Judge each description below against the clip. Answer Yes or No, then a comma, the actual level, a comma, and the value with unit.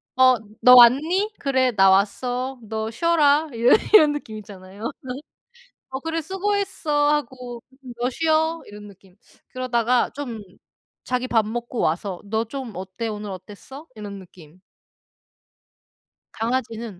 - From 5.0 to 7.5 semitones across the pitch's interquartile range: Yes, average, 5.3 semitones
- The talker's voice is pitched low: No, high, 245 Hz